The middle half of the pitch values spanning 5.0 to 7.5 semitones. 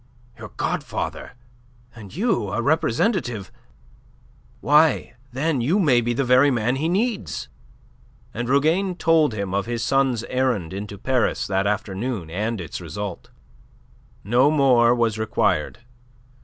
Yes: average, 5.3 semitones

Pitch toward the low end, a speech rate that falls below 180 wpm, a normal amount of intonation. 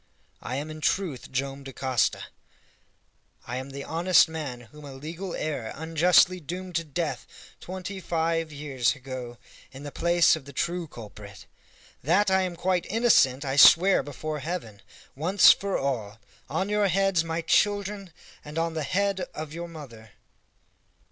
No: medium, 160 Hz; average, 155 wpm; average, 4.9 semitones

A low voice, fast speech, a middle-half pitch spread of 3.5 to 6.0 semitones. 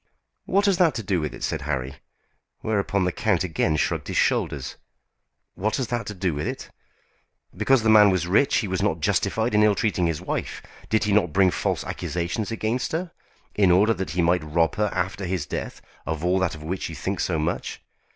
Yes: very low, 95 Hz; fast, 210 wpm; average, 4.3 semitones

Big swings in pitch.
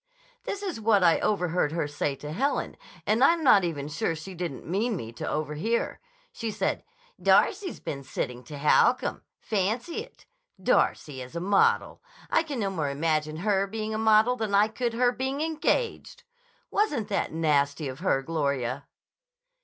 Yes: wide, 7.2 semitones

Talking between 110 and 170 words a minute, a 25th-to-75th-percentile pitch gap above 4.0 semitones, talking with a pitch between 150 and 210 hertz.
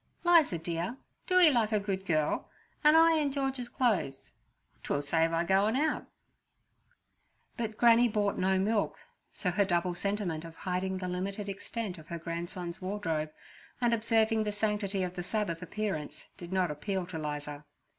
Yes: average, 165 wpm; average, 4.4 semitones; high, 190 Hz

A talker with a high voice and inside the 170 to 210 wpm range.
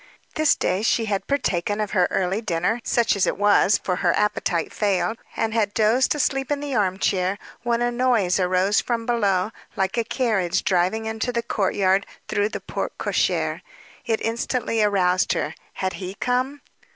Yes: high, 210 Hz; average, 175 wpm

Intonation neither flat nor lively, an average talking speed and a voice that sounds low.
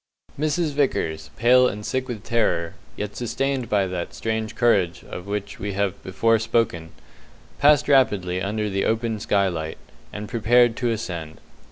Yes: average, 4.2 semitones; average, 150 wpm; low, 105 Hz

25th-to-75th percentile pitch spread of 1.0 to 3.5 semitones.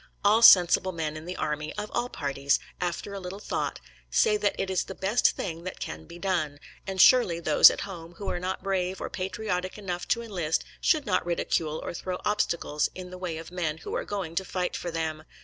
Yes: average, 3.0 semitones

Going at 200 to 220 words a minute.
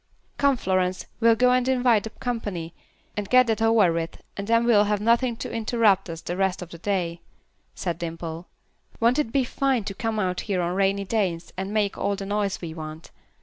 Yes: fast, 205 wpm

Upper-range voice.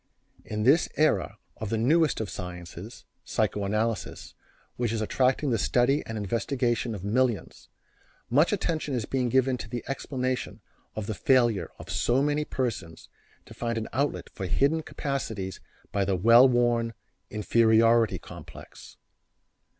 No: low, 115 Hz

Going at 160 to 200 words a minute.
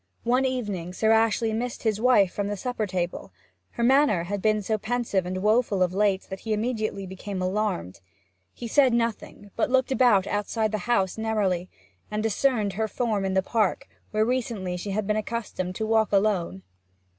Yes: average, 180 wpm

